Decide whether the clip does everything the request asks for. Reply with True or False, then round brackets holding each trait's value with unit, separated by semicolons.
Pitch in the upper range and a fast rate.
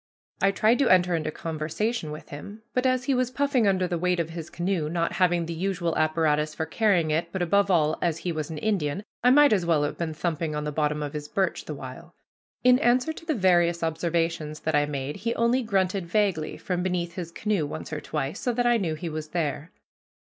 False (170 Hz; 225 wpm)